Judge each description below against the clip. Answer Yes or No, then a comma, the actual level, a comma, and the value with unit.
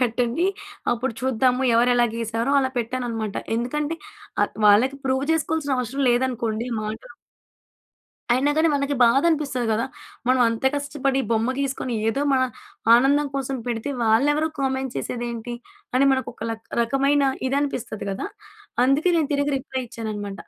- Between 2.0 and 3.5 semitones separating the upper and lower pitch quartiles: Yes, average, 3.2 semitones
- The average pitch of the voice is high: Yes, very high, 260 Hz